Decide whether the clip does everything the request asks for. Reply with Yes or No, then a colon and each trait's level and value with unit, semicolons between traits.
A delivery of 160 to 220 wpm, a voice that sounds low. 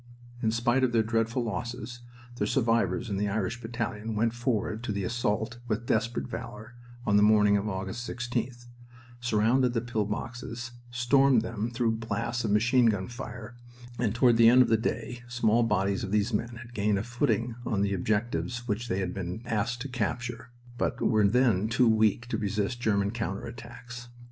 Yes: average, 185 wpm; low, 115 Hz